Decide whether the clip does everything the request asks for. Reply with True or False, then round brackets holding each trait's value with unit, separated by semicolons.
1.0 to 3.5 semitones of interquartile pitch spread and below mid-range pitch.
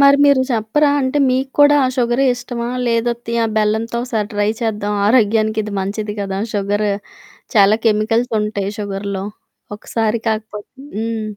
False (2.4 semitones; 220 Hz)